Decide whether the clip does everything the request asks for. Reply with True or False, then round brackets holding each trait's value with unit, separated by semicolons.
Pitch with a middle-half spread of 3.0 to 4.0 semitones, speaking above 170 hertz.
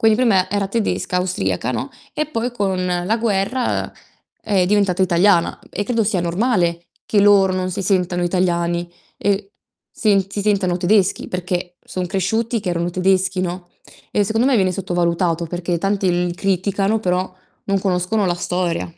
False (2.5 semitones; 185 Hz)